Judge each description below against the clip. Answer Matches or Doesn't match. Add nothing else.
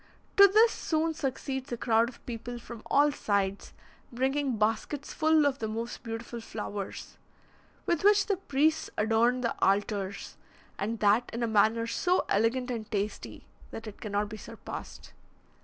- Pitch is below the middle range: Doesn't match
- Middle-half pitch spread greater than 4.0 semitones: Matches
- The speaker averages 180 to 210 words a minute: Doesn't match